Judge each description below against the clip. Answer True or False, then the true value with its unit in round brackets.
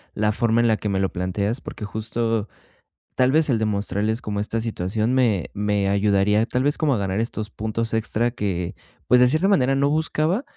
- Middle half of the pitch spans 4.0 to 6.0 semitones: False (3.4 semitones)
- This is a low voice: True (110 Hz)